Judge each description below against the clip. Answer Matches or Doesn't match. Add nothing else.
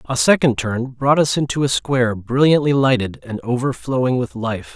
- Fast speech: Doesn't match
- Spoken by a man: Matches